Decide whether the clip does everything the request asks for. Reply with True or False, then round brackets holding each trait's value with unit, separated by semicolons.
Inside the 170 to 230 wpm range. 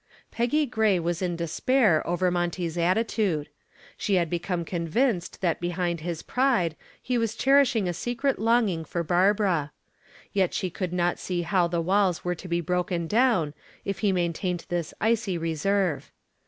False (155 wpm)